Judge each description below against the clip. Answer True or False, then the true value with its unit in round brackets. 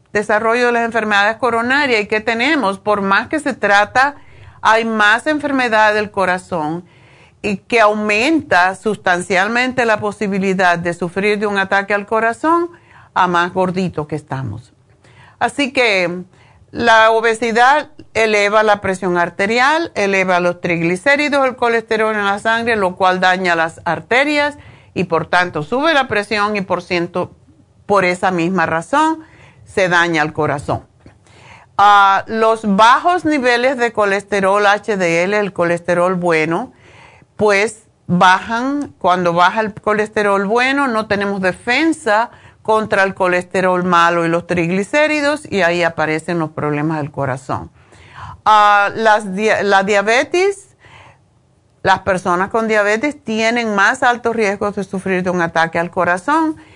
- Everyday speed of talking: True (135 wpm)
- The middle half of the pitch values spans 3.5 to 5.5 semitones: True (4.2 semitones)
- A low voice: False (200 Hz)